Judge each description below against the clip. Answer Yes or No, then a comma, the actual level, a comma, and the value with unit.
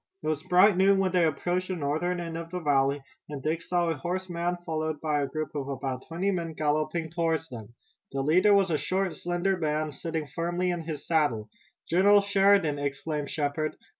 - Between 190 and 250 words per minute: Yes, average, 195 wpm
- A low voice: No, medium, 165 Hz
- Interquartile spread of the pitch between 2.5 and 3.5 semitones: Yes, average, 3.2 semitones